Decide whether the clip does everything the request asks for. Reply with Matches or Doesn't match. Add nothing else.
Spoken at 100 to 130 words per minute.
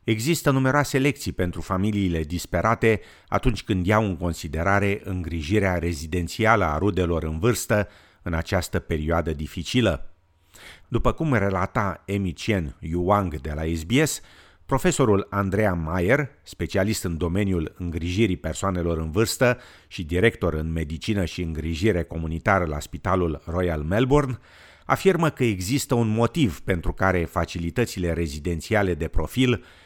Matches